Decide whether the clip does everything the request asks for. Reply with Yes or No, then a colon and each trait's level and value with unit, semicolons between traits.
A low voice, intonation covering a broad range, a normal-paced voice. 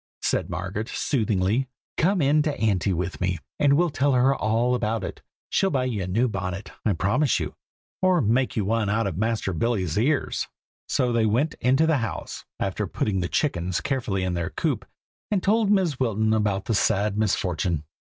Yes: low, 110 Hz; wide, 5.7 semitones; average, 185 wpm